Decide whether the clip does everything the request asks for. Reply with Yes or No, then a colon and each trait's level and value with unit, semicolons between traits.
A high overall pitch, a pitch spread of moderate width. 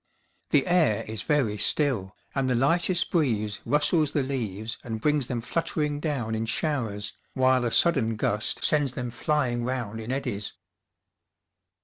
No: low, 125 Hz; average, 4.9 semitones